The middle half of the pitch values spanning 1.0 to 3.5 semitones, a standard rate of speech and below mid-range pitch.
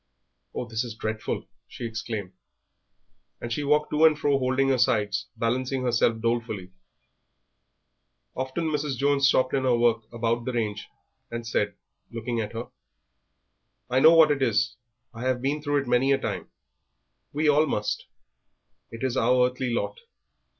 Yes: average, 3.0 semitones; average, 155 wpm; low, 125 Hz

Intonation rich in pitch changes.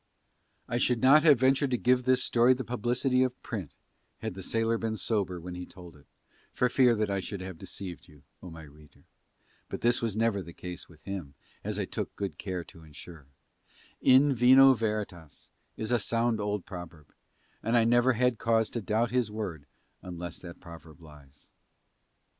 Yes: wide, 5.7 semitones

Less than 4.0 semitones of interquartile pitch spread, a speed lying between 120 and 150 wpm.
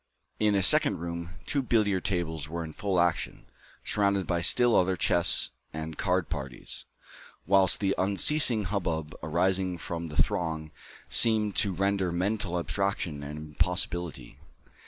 Yes: average, 3.5 semitones; slow, 135 wpm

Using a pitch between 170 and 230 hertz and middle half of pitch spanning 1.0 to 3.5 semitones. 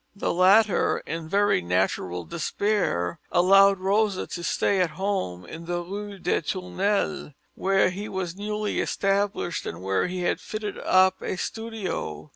Yes: medium, 185 Hz; average, 3.2 semitones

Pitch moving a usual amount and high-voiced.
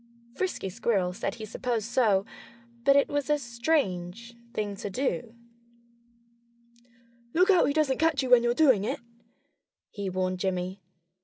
No: wide, 6.3 semitones; high, 235 Hz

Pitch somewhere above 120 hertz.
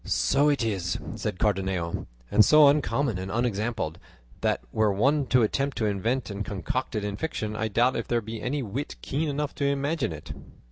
No: low, 115 Hz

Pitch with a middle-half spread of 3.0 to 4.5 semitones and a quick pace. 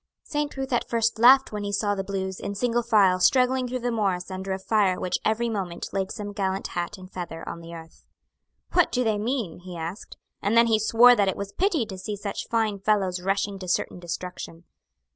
Yes: average, 3.7 semitones; fast, 220 wpm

